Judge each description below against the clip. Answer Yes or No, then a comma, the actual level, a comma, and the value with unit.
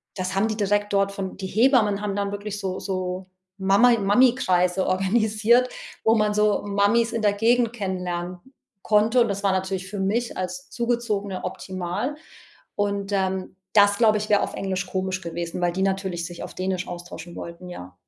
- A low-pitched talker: No, high, 200 Hz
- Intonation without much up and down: Yes, narrow, 2.3 semitones